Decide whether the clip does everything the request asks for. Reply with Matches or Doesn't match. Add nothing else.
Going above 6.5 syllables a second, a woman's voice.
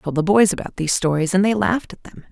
Matches